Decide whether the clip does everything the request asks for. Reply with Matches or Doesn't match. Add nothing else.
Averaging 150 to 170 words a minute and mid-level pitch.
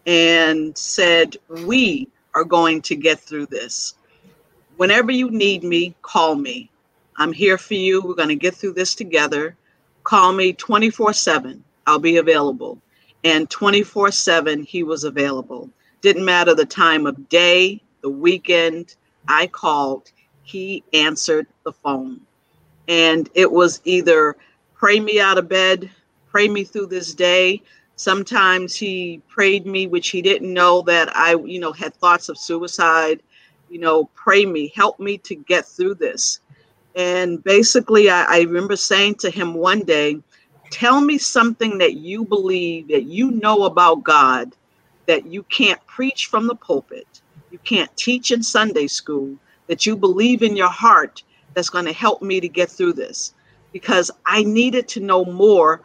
Matches